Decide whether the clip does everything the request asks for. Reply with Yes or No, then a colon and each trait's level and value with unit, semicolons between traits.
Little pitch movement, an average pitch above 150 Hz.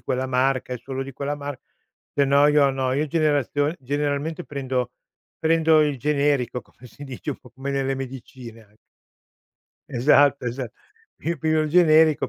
No: narrow, 2.3 semitones; medium, 140 Hz